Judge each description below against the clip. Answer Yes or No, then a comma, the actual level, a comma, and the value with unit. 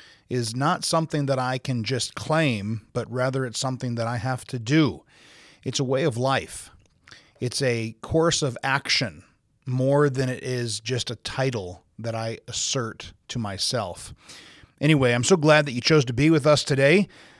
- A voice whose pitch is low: Yes, low, 130 Hz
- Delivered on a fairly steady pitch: No, average, 3.4 semitones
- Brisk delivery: No, average, 175 wpm